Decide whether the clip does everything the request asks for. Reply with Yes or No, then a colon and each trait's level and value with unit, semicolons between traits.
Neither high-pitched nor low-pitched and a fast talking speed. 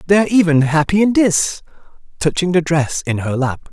No: medium, 165 Hz; average, 175 wpm